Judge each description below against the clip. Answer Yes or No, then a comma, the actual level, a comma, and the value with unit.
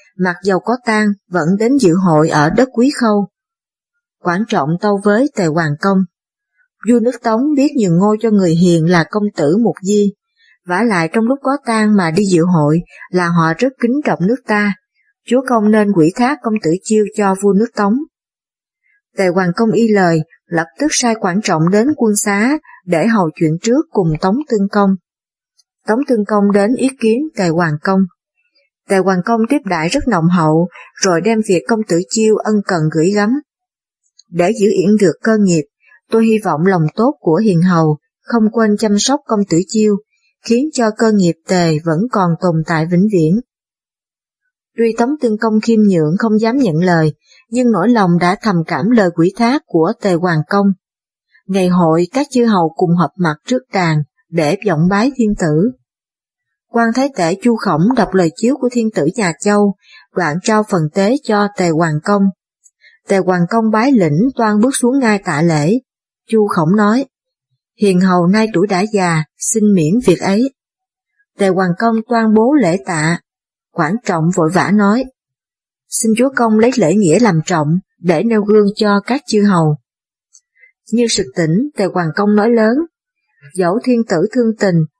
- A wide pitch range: No, average, 4.8 semitones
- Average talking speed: Yes, average, 185 wpm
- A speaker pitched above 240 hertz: No, high, 205 Hz